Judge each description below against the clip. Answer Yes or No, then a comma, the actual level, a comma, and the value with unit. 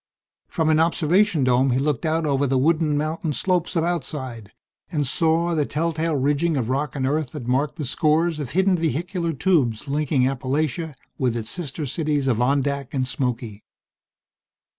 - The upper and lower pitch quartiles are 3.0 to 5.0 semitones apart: Yes, average, 3.8 semitones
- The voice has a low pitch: No, medium, 150 Hz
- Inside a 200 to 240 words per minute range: No, average, 165 wpm